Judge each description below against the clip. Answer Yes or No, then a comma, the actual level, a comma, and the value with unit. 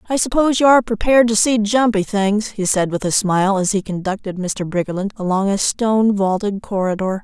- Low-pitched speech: No, high, 205 Hz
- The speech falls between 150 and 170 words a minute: No, average, 200 wpm